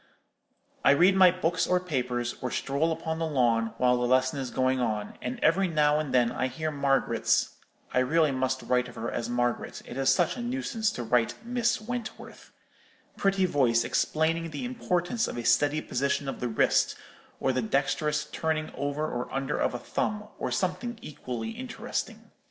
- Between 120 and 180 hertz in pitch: Yes, medium, 140 Hz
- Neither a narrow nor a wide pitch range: No, wide, 5.8 semitones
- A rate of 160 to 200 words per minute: Yes, average, 175 wpm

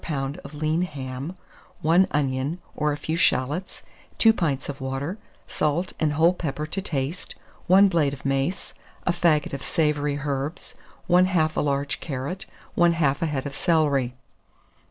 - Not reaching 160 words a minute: Yes, average, 150 wpm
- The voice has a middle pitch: Yes, medium, 150 Hz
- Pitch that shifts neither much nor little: Yes, average, 3.7 semitones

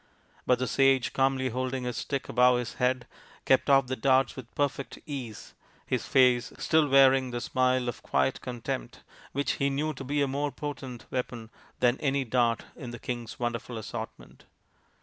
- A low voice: Yes, low, 130 Hz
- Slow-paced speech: No, average, 170 wpm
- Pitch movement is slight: Yes, narrow, 2.0 semitones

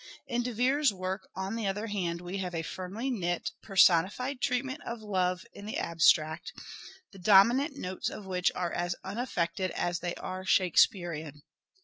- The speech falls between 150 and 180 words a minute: Yes, average, 160 wpm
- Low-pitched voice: No, high, 190 Hz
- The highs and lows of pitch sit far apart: No, average, 4.2 semitones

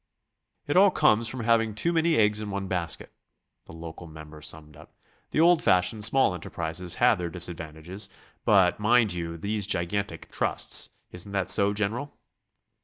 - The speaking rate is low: No, average, 160 wpm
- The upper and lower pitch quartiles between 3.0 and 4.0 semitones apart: No, average, 4.6 semitones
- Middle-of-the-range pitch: No, low, 100 Hz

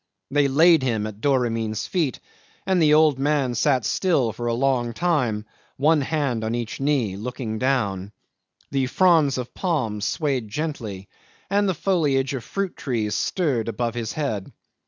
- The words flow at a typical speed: Yes, average, 155 wpm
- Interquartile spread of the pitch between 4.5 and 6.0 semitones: Yes, average, 5.0 semitones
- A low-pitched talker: Yes, low, 130 Hz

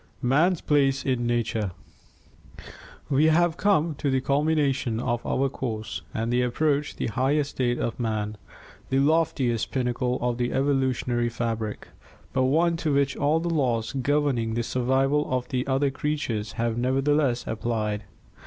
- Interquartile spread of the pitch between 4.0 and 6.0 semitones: No, average, 3.5 semitones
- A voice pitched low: Yes, low, 130 Hz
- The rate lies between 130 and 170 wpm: Yes, average, 145 wpm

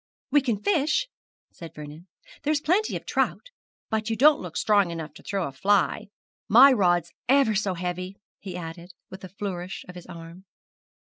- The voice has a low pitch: No, high, 190 Hz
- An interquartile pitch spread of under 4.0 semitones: No, average, 5.2 semitones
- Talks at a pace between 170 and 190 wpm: Yes, average, 175 wpm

